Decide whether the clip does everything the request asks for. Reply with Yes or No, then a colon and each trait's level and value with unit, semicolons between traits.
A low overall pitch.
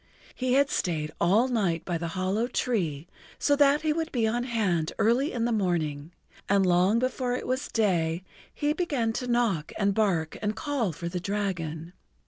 No: high, 210 Hz